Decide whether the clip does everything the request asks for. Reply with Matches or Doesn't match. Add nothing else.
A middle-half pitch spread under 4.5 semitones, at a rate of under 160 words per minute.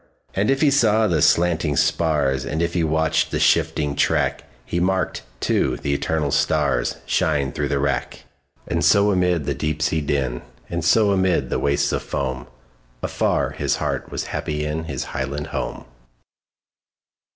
Matches